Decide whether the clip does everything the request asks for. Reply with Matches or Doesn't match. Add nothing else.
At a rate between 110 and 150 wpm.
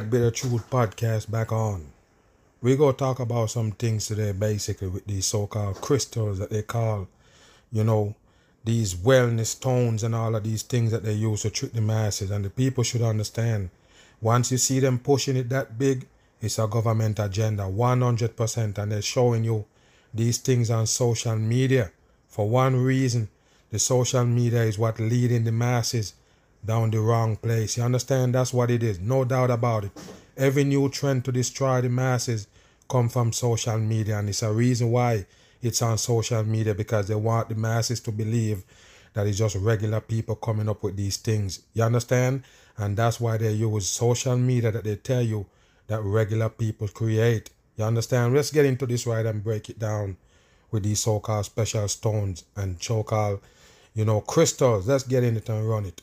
Doesn't match